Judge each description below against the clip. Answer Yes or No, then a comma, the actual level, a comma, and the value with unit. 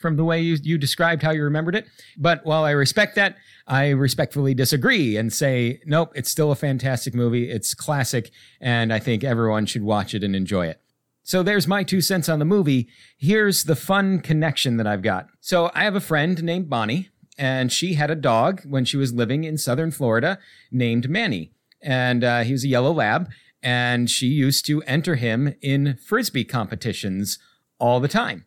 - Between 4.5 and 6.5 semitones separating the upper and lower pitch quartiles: Yes, average, 5.3 semitones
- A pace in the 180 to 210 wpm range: Yes, average, 195 wpm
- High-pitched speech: No, medium, 140 Hz